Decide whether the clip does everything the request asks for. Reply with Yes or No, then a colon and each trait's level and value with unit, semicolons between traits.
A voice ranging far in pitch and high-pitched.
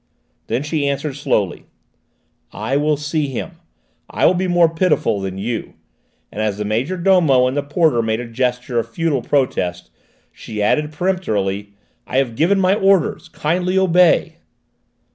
No: wide, 6.8 semitones; medium, 140 Hz